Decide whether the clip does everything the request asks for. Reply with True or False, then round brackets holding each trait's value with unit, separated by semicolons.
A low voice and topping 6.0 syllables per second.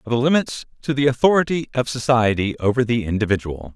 True (120 Hz; 6.2 syllables/s)